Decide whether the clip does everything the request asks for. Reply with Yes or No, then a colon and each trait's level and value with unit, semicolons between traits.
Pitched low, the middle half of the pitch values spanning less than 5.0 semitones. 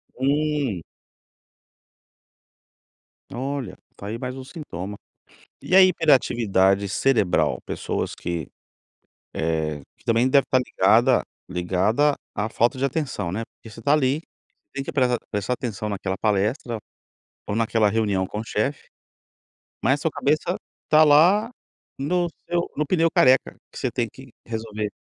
No: low, 120 Hz; wide, 5.6 semitones